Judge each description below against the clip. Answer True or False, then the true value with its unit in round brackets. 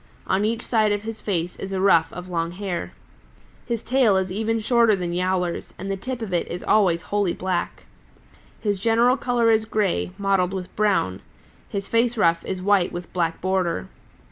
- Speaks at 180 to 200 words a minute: True (185 wpm)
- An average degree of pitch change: True (3.5 semitones)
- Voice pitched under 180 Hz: False (195 Hz)